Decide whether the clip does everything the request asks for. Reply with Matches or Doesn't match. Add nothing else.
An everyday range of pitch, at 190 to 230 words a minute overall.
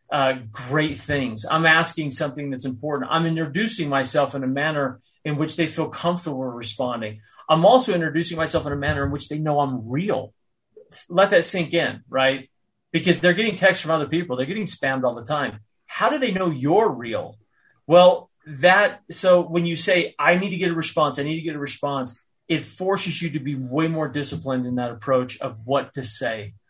Matches